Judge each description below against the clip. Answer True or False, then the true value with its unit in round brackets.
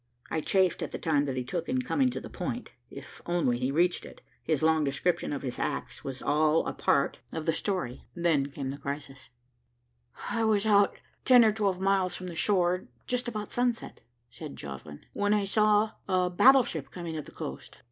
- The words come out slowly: False (195 wpm)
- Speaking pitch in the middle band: True (175 Hz)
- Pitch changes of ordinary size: False (6.2 semitones)